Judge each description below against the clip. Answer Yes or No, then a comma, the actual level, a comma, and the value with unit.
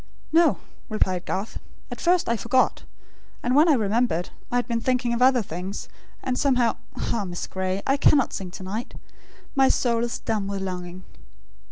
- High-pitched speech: Yes, high, 230 Hz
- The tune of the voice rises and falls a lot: No, average, 4.8 semitones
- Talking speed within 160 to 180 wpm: Yes, average, 175 wpm